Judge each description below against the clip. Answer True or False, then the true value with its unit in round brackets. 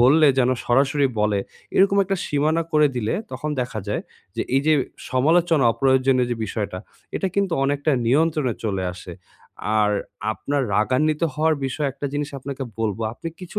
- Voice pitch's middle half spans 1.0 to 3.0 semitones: False (4.2 semitones)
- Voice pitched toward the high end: False (140 Hz)